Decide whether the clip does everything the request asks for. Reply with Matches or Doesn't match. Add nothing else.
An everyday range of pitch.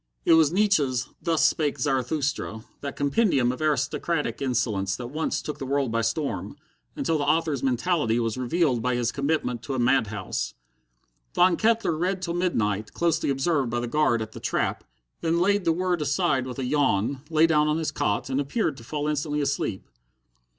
Matches